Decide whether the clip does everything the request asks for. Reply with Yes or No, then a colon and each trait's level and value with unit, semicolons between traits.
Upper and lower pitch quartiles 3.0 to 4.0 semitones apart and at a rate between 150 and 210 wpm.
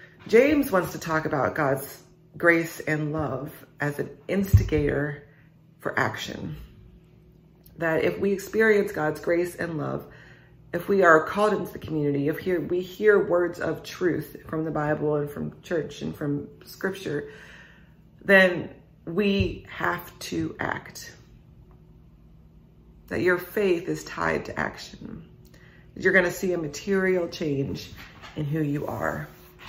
No: average, 3.5 semitones; average, 140 wpm